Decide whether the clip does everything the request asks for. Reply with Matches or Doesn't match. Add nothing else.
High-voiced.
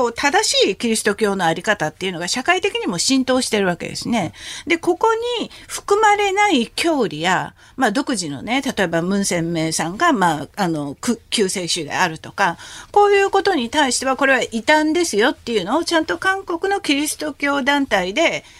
Matches